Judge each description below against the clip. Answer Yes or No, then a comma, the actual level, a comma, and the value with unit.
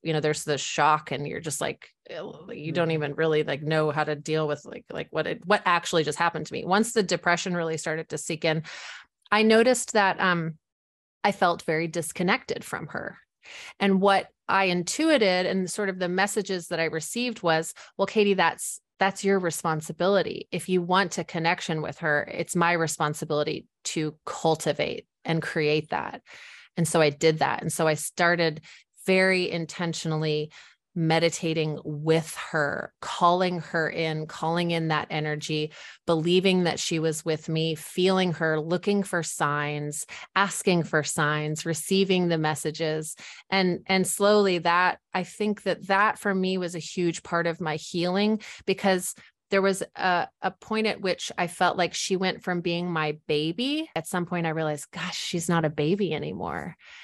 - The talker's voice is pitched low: No, medium, 170 Hz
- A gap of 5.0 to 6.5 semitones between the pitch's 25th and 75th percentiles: No, average, 3.1 semitones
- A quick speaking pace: No, average, 175 wpm